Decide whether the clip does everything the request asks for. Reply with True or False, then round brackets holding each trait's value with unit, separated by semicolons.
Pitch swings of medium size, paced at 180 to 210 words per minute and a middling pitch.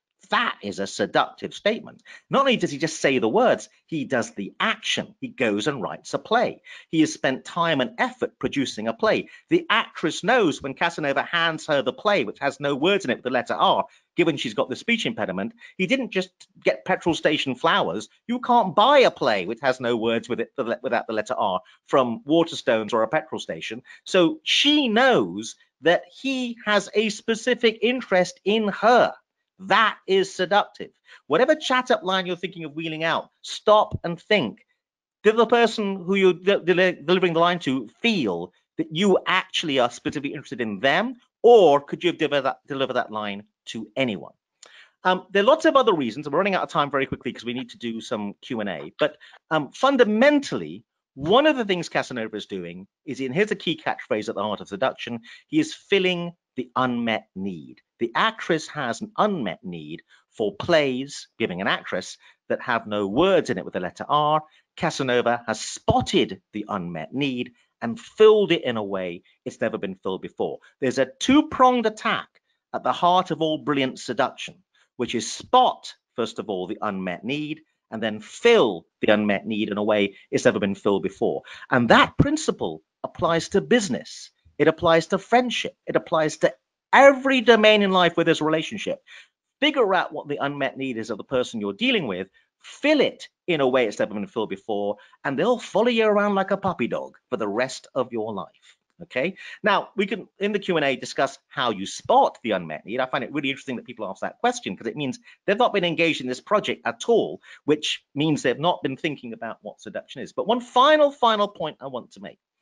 False (8.6 semitones; 200 wpm; 170 Hz)